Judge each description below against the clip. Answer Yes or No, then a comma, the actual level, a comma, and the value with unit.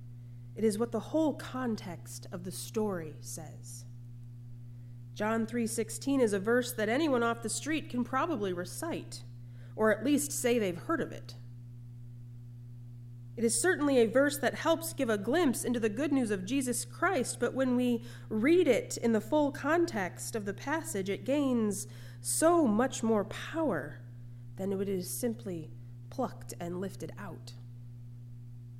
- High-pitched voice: Yes, high, 195 Hz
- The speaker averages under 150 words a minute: No, average, 155 wpm